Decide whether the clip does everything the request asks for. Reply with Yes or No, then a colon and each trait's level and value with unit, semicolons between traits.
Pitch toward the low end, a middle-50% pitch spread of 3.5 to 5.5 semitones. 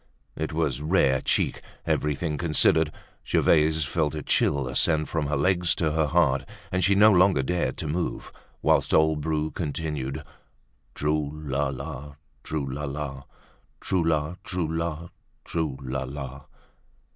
No: very low, 75 Hz; narrow, 2.4 semitones